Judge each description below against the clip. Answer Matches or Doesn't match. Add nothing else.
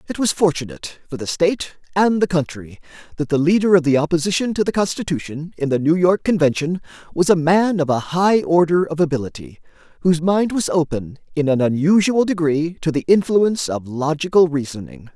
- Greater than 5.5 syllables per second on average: Matches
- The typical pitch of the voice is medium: Matches